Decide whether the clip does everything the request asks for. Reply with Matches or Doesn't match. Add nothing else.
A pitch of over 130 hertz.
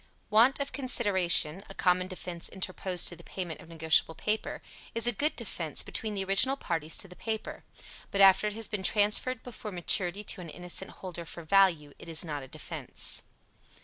Matches